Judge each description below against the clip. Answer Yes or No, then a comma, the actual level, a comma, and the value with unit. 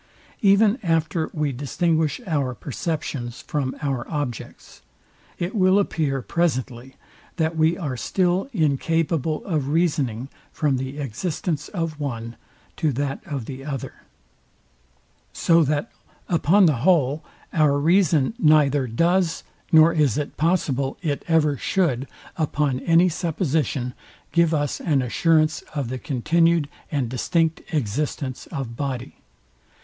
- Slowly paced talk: Yes, slow, 125 wpm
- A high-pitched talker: No, medium, 150 Hz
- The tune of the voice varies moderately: Yes, average, 3.7 semitones